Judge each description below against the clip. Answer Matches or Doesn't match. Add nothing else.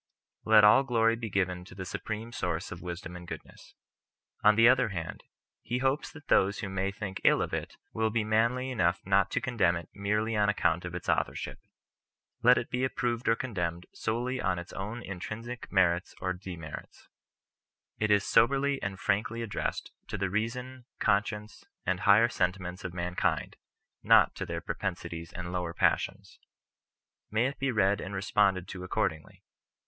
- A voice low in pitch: Matches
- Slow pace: Doesn't match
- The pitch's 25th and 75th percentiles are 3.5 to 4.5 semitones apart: Matches